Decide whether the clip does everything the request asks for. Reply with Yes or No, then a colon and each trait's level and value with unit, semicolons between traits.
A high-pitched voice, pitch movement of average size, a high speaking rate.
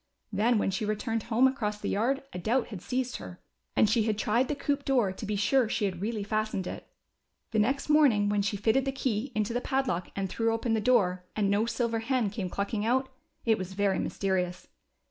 Yes: high, 220 Hz; average, 3.6 semitones; fast, 225 wpm